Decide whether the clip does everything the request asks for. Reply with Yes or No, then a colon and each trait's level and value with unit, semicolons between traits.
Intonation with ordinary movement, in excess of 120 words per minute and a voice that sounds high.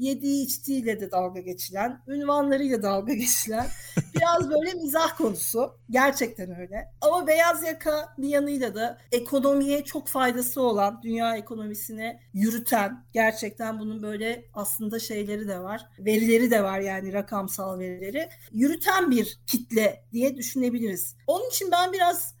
Yes: average, 4.7 semitones; average, 130 wpm; high, 235 Hz